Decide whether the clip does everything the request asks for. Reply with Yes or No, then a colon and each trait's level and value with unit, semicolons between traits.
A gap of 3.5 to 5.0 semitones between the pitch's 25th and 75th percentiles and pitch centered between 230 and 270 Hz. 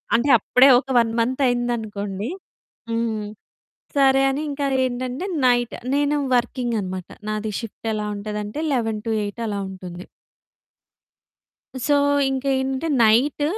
Yes: average, 3.9 semitones; high, 235 Hz